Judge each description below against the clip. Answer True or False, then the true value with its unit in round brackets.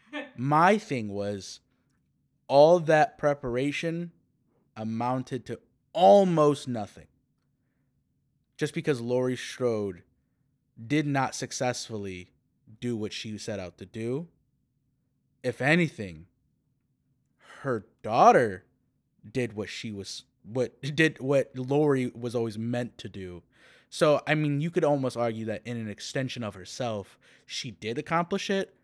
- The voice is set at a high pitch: False (125 Hz)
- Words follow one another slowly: True (120 wpm)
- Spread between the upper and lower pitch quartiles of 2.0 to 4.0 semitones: False (4.5 semitones)